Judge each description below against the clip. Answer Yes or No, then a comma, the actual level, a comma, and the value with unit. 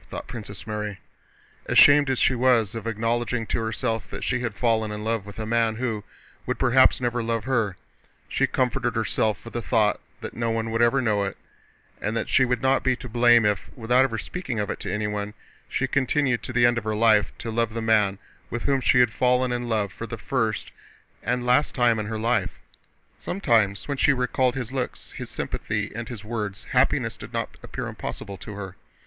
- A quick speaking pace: Yes, fast, 210 wpm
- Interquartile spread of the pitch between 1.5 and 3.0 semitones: Yes, narrow, 2.5 semitones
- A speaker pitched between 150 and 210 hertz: No, low, 115 Hz